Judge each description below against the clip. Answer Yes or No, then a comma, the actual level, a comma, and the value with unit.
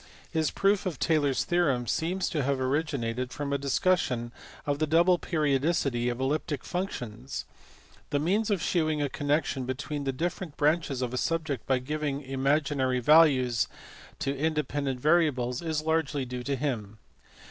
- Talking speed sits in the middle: Yes, average, 150 wpm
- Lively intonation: No, average, 3.6 semitones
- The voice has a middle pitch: Yes, medium, 145 Hz